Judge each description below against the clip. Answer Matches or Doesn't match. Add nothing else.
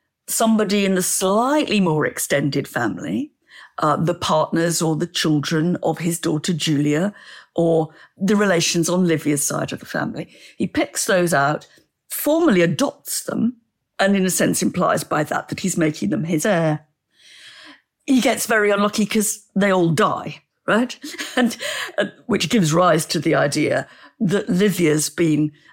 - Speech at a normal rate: Matches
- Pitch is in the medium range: Matches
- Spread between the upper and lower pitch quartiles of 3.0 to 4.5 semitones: Doesn't match